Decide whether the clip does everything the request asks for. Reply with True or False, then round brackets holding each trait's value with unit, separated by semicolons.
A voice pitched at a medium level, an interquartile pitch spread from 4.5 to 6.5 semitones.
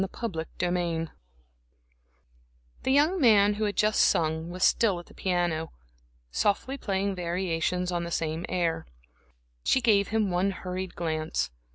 False (180 Hz; 3.4 semitones)